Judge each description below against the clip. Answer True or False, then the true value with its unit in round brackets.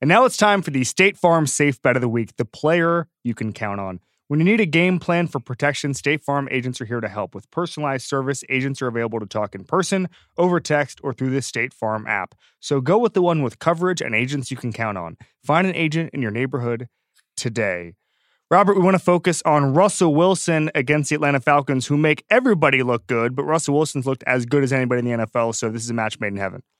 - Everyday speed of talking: False (240 wpm)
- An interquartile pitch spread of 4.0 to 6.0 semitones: True (5.4 semitones)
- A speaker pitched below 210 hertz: True (140 Hz)